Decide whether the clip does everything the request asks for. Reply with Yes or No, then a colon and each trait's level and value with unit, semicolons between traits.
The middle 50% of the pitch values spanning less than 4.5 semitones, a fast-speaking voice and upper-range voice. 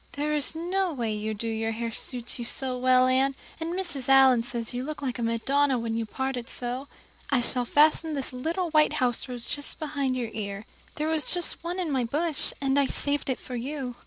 Yes: average, 3.9 semitones; fast, 220 wpm; very high, 265 Hz